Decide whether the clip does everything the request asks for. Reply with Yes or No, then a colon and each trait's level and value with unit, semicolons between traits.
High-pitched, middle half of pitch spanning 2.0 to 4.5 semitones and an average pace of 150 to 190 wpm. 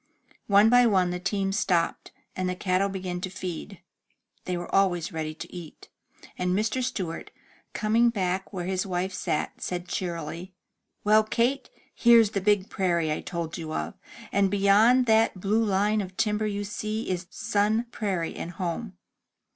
Yes: high, 195 Hz; average, 3.0 semitones; average, 165 wpm